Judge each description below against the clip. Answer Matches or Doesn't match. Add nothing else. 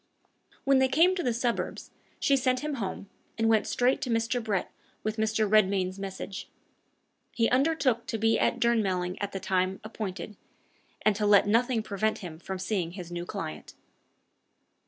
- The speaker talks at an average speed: Matches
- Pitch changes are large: Doesn't match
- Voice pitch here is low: Doesn't match